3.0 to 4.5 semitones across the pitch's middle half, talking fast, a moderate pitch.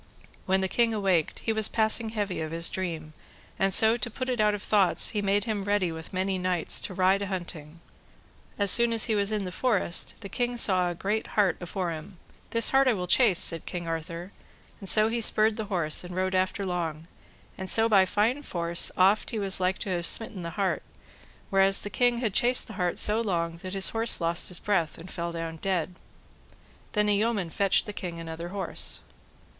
No: average, 3.5 semitones; fast, 215 wpm; high, 195 Hz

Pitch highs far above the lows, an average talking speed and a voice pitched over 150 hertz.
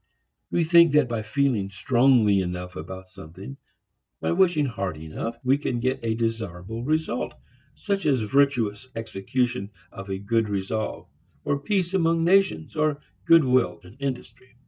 No: wide, 6.2 semitones; average, 145 wpm; low, 120 Hz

